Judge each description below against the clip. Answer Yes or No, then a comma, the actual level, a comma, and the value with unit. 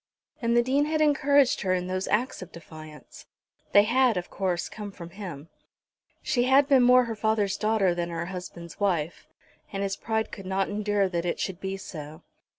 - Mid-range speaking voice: No, high, 195 Hz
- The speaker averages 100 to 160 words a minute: No, average, 190 wpm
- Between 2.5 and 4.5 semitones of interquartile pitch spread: No, average, 4.9 semitones